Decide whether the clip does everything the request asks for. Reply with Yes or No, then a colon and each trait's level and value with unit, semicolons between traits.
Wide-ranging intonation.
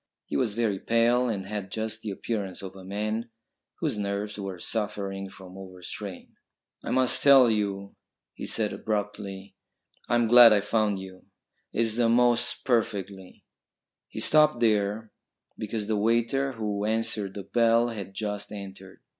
No: average, 2.7 semitones